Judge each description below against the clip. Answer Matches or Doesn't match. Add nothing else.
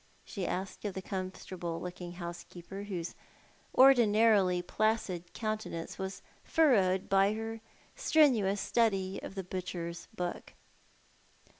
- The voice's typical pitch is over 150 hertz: Matches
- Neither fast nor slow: Doesn't match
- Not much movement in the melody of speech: Doesn't match